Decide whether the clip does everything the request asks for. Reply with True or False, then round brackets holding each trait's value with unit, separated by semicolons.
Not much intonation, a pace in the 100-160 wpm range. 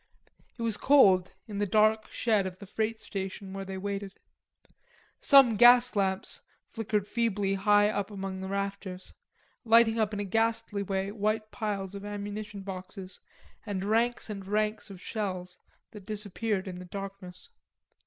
True (2.1 semitones; 155 wpm)